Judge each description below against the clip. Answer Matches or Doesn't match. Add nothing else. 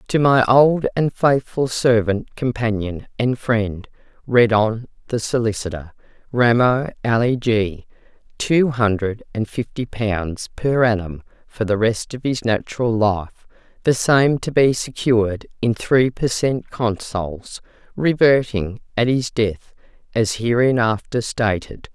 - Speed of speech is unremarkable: Doesn't match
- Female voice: Matches